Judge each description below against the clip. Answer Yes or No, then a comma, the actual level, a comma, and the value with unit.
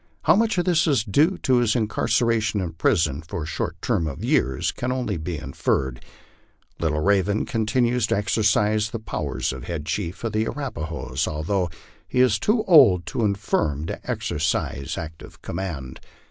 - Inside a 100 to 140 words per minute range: No, average, 175 wpm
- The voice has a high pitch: No, low, 100 Hz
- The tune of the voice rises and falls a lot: Yes, wide, 7.0 semitones